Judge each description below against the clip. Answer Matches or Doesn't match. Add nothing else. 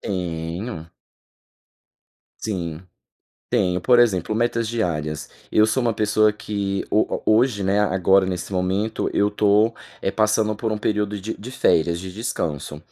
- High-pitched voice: Doesn't match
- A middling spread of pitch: Matches